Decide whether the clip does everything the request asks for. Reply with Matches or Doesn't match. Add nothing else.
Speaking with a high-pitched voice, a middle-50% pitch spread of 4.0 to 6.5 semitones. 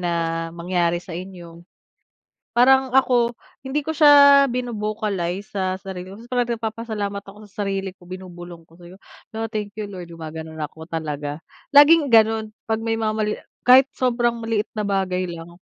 Matches